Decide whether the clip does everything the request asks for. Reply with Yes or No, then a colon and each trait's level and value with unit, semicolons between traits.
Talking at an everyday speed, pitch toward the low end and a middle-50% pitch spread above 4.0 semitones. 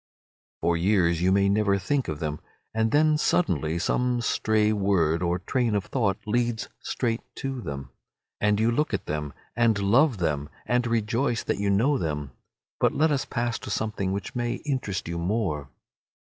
Yes: average, 175 wpm; low, 105 Hz; wide, 5.5 semitones